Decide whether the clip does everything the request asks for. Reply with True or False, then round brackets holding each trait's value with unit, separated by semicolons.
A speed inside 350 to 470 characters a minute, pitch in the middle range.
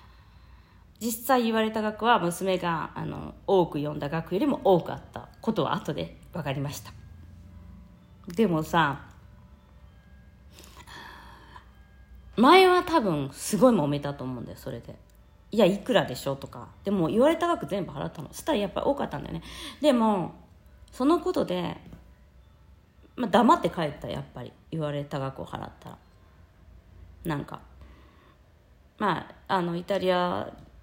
False (265 characters per minute; 145 Hz)